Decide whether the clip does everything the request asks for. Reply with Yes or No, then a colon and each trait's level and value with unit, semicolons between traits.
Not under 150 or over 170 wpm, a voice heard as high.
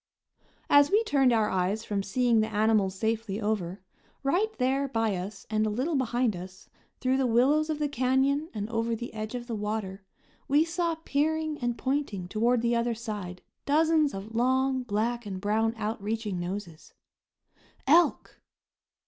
Yes: average, 160 wpm; high, 230 Hz